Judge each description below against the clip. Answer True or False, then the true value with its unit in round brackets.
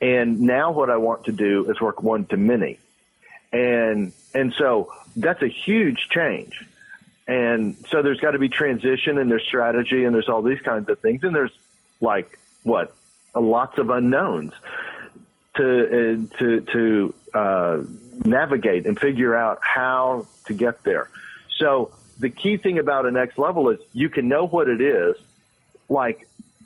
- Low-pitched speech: True (125 Hz)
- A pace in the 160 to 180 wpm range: True (165 wpm)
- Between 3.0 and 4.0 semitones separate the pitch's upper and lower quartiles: True (3.4 semitones)